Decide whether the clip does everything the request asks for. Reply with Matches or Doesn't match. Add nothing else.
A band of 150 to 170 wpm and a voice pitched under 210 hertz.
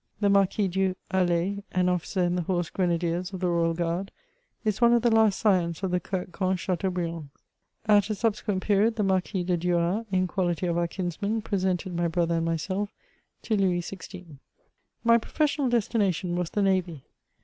Doesn't match